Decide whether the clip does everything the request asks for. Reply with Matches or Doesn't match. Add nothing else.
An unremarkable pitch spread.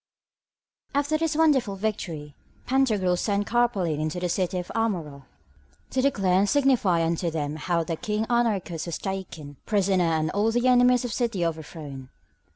Doesn't match